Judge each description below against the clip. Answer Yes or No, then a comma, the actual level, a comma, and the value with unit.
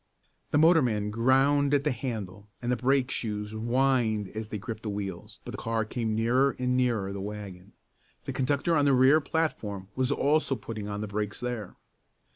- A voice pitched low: Yes, low, 115 Hz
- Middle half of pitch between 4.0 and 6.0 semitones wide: Yes, average, 4.3 semitones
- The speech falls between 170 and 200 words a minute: Yes, average, 185 wpm